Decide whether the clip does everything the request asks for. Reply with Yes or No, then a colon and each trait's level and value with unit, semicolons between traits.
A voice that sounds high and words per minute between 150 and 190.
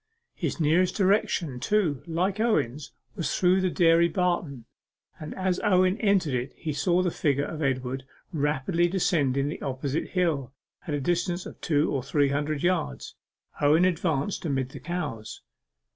No: medium, 160 Hz; average, 155 wpm